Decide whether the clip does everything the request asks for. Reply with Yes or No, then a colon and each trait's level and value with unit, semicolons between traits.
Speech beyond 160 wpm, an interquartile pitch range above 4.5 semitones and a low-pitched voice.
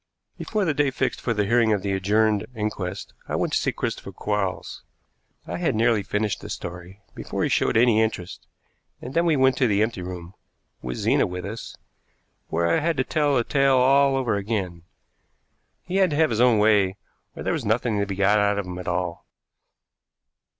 Yes: average, 200 wpm; average, 4.9 semitones; low, 105 Hz